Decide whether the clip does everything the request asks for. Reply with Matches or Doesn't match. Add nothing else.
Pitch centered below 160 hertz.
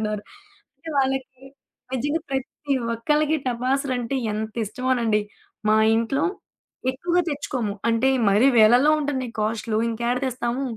Doesn't match